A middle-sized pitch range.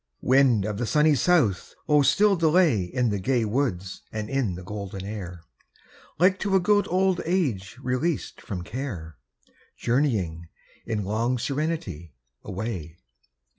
No: wide, 7.6 semitones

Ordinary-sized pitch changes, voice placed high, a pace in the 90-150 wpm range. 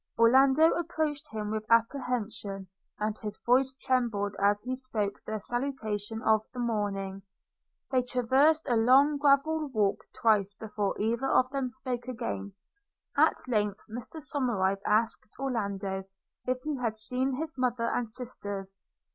Yes: average, 4.0 semitones; high, 235 Hz; average, 140 wpm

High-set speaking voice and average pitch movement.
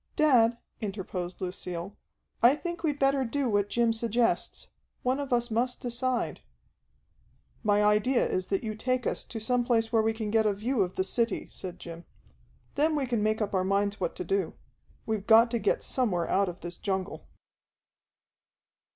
Yes: high, 225 Hz; average, 3.8 semitones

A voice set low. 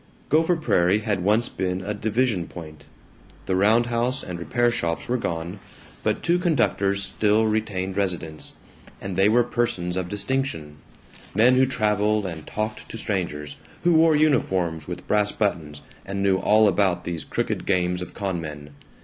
Yes: low, 100 Hz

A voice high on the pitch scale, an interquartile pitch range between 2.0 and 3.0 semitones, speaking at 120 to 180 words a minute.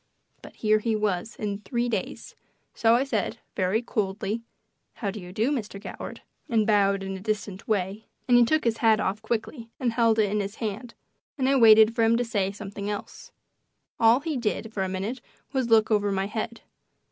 No: high, 220 Hz; narrow, 2.5 semitones; fast, 205 wpm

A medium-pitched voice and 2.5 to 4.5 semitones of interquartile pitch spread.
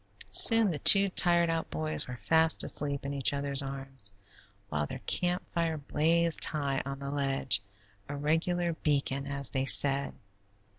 Yes: medium, 145 Hz; average, 3.2 semitones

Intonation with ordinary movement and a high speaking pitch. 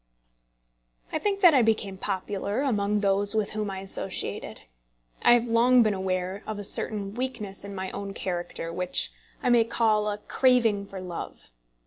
Yes: average, 3.0 semitones; high, 205 Hz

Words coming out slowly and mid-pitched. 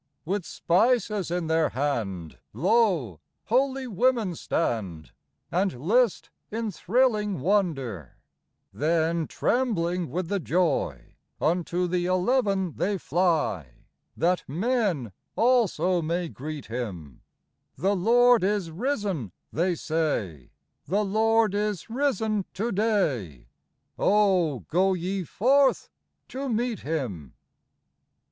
Yes: slow, 110 wpm; medium, 180 Hz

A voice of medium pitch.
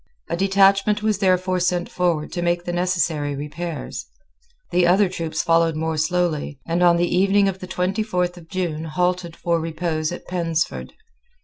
Yes: medium, 175 Hz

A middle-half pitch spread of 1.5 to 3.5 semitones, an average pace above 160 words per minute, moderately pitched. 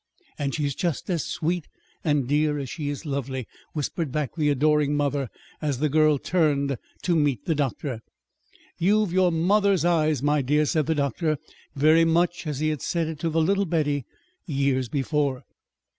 Yes: narrow, 2.6 semitones; average, 175 wpm; medium, 150 Hz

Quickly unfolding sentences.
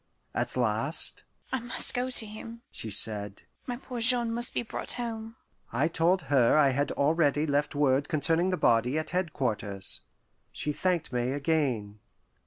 No: average, 160 wpm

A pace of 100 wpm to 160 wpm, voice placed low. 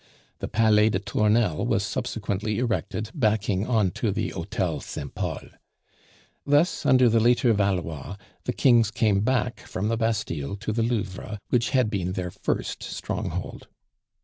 Yes: average, 150 wpm; low, 110 Hz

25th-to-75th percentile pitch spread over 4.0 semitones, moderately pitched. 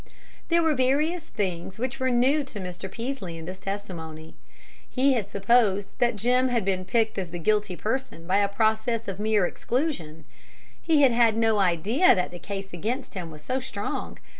No: wide, 5.4 semitones; high, 215 Hz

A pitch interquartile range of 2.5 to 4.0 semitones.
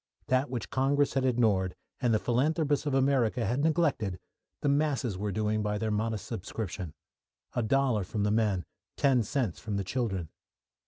No: average, 4.6 semitones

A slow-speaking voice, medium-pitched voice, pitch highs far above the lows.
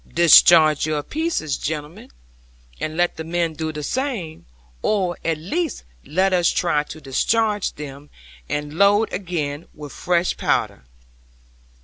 No: slow, 130 wpm; medium, 165 Hz; average, 3.8 semitones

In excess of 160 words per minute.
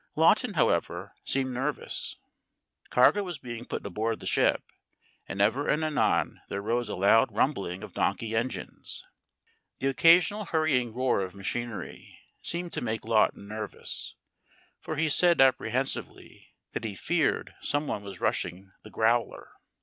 No: average, 140 wpm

